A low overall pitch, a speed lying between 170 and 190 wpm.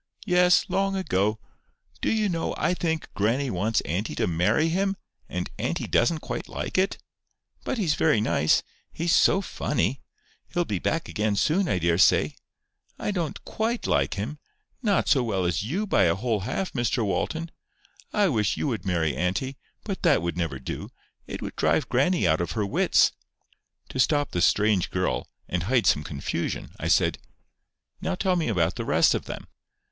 Yes: low, 125 Hz; average, 175 wpm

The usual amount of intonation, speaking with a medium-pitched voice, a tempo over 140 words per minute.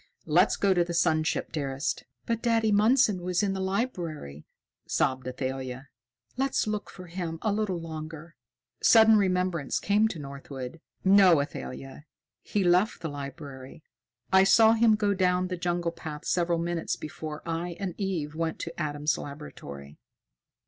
Yes: average, 4.6 semitones; medium, 170 Hz; average, 150 wpm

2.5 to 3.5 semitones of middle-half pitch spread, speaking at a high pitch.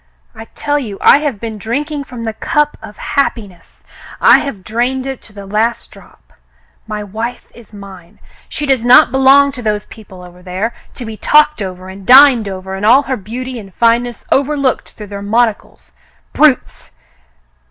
No: average, 4.6 semitones; high, 230 Hz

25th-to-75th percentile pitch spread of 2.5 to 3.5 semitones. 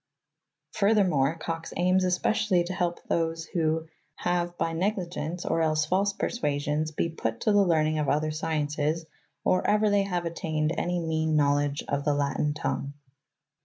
Yes: average, 2.9 semitones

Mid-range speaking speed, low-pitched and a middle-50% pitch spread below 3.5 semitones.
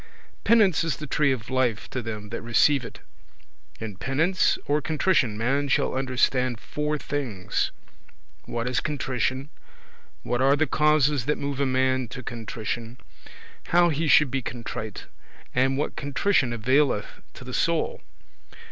No: average, 145 wpm; low, 130 Hz; average, 3.9 semitones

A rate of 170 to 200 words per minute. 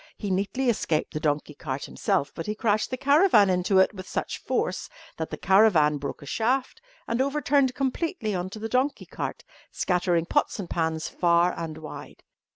Yes: average, 180 wpm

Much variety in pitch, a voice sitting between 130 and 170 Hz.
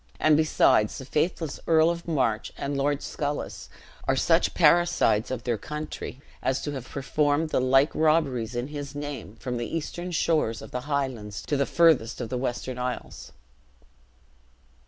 No: average, 3.7 semitones; medium, 140 Hz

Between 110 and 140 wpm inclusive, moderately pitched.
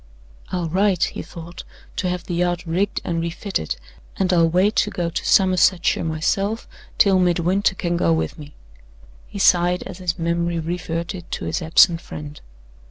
No: average, 165 wpm; medium, 175 Hz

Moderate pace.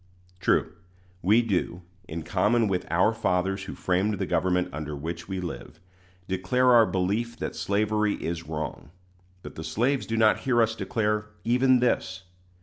Yes: average, 155 wpm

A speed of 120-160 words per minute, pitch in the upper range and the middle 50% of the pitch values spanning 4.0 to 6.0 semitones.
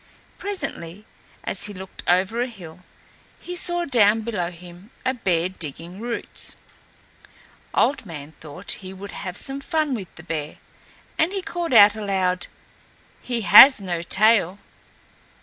Yes: average, 140 wpm; high, 200 Hz; wide, 5.6 semitones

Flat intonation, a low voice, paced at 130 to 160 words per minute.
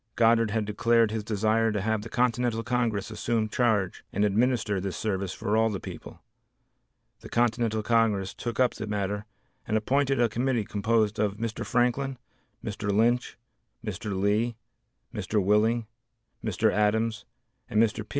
Yes: narrow, 2.0 semitones; low, 110 Hz; average, 150 wpm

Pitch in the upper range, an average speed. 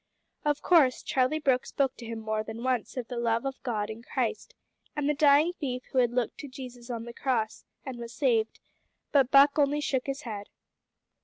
No: very high, 255 Hz; fast, 210 wpm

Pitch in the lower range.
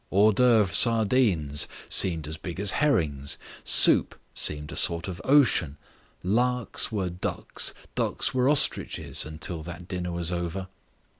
Yes: very low, 90 Hz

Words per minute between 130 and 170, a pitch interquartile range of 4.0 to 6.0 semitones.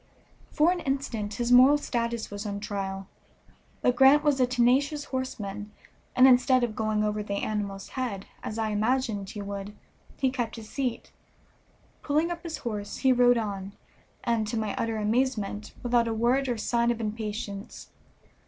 No: average, 165 wpm; average, 3.6 semitones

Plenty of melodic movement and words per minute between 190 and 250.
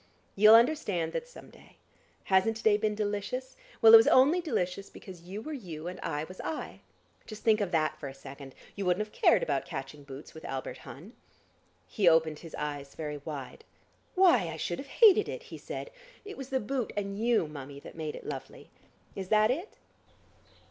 Yes: wide, 6.7 semitones; average, 195 wpm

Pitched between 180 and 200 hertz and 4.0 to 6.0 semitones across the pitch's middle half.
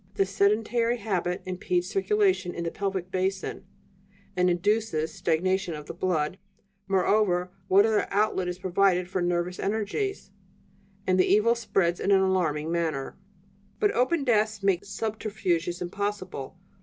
No: high, 190 Hz; average, 2.9 semitones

